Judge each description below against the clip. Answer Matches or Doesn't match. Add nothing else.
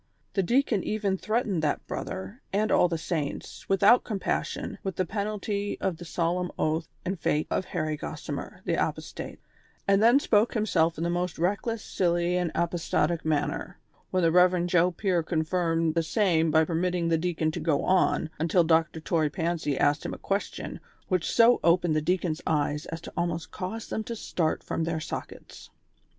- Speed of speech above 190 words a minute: Doesn't match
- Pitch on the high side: Doesn't match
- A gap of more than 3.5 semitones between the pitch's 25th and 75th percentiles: Doesn't match